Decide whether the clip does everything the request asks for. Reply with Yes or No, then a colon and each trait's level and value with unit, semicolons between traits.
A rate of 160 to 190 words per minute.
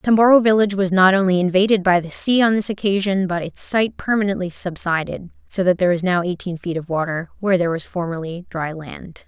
No: fast, 205 wpm